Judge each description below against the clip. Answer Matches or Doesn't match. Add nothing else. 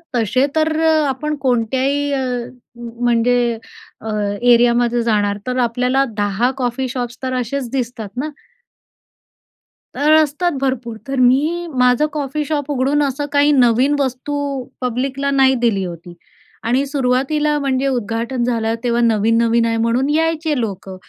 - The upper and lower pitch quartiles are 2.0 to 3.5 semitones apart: Matches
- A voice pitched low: Doesn't match